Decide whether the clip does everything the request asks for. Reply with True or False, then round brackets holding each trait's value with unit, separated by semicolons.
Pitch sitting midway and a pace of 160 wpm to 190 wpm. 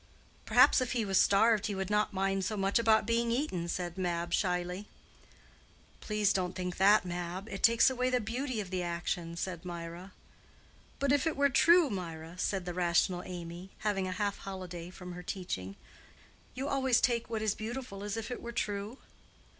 False (195 Hz; 185 wpm)